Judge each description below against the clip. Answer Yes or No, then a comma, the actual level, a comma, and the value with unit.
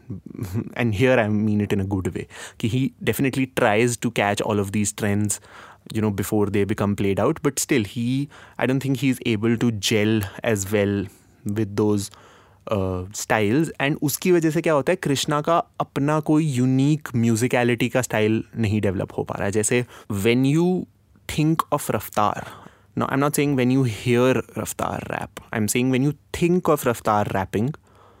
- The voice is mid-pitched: No, low, 120 Hz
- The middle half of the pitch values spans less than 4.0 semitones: No, average, 4.6 semitones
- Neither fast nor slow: Yes, average, 180 wpm